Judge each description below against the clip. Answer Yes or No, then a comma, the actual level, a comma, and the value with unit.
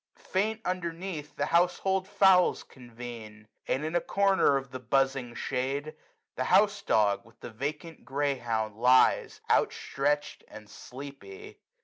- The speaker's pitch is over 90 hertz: Yes, low, 135 Hz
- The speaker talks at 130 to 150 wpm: Yes, average, 140 wpm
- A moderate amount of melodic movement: No, wide, 5.9 semitones